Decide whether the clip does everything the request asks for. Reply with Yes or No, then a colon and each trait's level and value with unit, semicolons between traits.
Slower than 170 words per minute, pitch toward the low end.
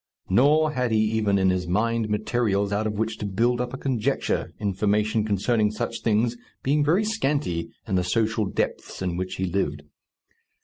No: average, 175 wpm; low, 110 Hz